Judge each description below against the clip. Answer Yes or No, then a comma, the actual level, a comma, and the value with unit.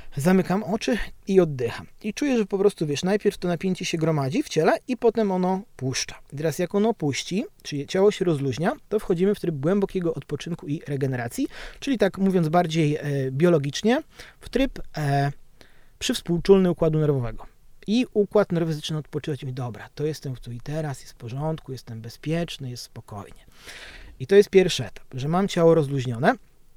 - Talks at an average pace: No, fast, 175 wpm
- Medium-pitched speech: Yes, medium, 165 Hz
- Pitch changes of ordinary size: No, wide, 5.8 semitones